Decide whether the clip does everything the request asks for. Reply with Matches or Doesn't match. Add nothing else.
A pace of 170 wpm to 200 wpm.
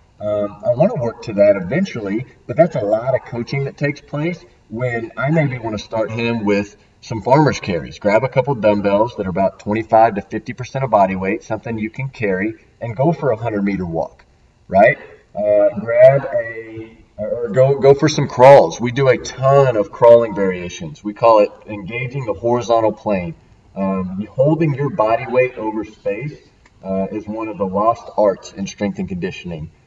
Matches